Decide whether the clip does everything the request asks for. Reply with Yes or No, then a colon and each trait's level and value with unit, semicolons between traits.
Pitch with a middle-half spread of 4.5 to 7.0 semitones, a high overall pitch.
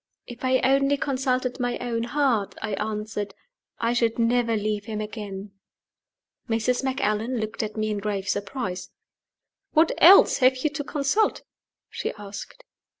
No: average, 3.7 semitones; high, 230 Hz